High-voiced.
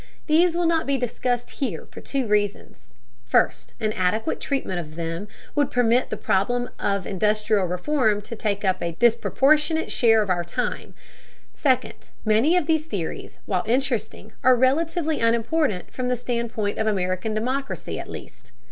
Yes: high, 230 Hz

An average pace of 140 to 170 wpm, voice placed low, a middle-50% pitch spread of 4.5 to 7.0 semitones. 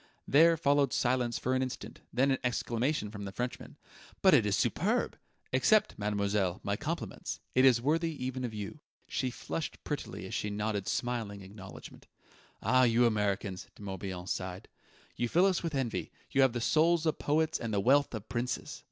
No: average, 180 wpm; low, 120 Hz; average, 5.2 semitones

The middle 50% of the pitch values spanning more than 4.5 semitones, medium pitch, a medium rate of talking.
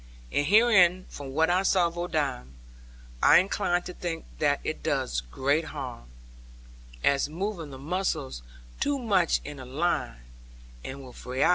Yes: average, 5.1 semitones; medium, 160 Hz; average, 150 wpm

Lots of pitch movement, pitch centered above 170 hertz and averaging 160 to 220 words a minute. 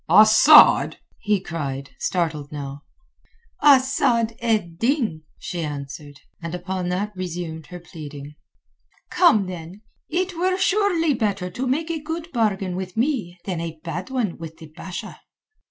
No: wide, 7.5 semitones; medium, 185 Hz; average, 140 wpm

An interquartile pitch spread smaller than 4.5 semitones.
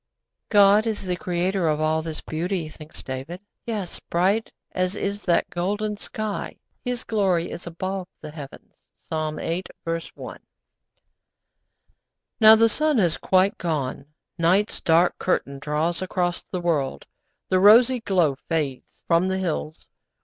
Yes: average, 3.9 semitones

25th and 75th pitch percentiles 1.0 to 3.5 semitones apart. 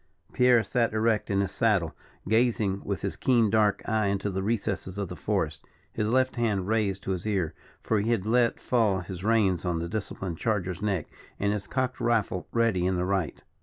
Yes: average, 3.1 semitones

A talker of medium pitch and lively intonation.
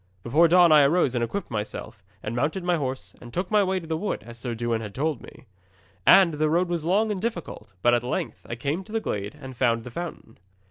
Yes: medium, 150 Hz; wide, 6.9 semitones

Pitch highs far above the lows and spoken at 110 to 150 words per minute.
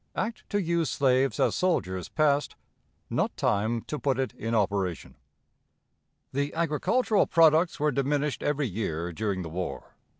Yes: wide, 7.2 semitones; average, 140 wpm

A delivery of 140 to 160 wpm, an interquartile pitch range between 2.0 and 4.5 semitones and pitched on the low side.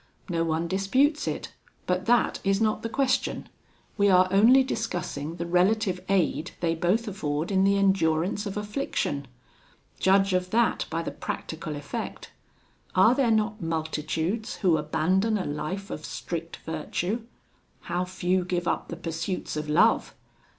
No: average, 150 wpm; average, 4.1 semitones; medium, 185 Hz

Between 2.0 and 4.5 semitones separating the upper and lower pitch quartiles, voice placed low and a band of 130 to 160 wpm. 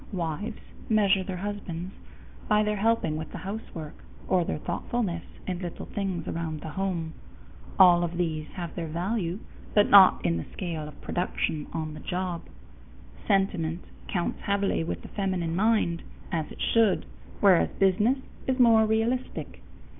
No: average, 3.7 semitones; medium, 185 Hz; average, 150 wpm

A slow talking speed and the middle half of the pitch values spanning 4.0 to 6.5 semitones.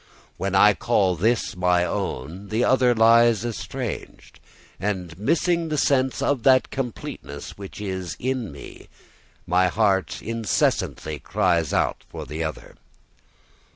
Yes: slow, 125 wpm; average, 5.1 semitones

